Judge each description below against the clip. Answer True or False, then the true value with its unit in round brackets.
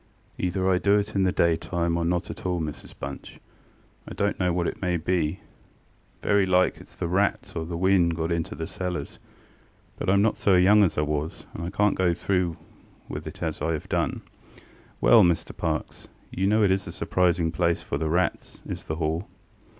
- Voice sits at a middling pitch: False (90 Hz)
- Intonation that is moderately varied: False (2.3 semitones)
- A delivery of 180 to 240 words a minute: True (205 wpm)